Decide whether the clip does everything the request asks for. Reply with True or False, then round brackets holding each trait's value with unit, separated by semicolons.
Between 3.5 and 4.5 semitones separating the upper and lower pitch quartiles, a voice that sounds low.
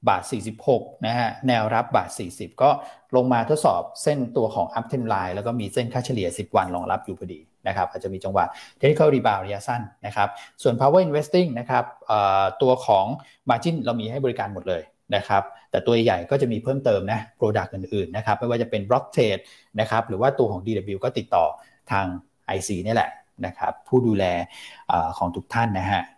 True (3.8 semitones; 115 Hz)